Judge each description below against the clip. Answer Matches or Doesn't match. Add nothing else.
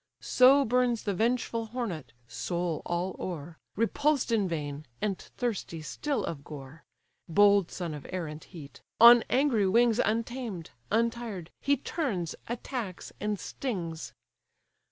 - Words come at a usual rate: Doesn't match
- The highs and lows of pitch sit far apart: Matches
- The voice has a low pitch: Doesn't match